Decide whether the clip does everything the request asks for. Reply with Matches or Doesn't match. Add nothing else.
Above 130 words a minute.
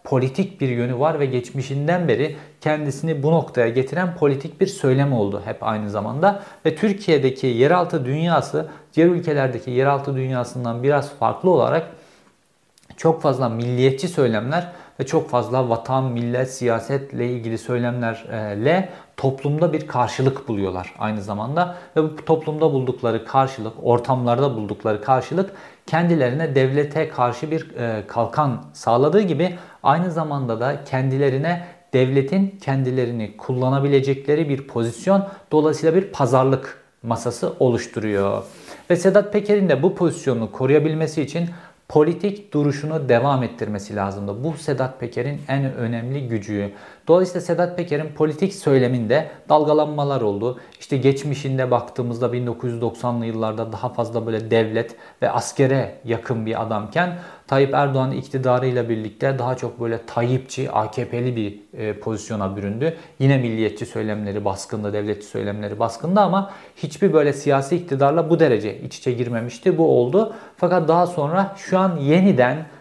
Doesn't match